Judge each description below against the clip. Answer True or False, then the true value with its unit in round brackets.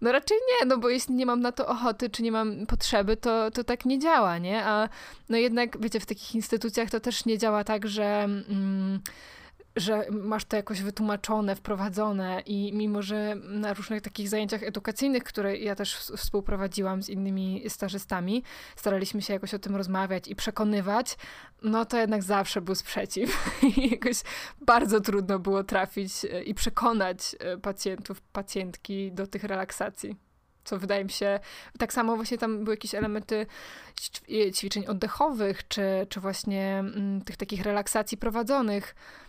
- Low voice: False (210 Hz)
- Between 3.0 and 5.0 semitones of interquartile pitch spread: False (2.4 semitones)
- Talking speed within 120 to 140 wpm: False (155 wpm)